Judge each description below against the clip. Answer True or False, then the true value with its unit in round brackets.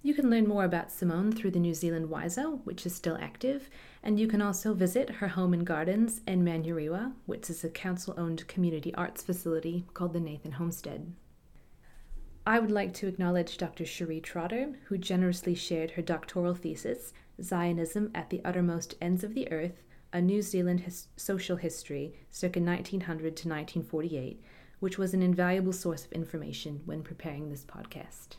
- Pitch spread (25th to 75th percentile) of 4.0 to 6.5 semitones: False (2.6 semitones)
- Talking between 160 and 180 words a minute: True (170 wpm)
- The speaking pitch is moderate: True (175 Hz)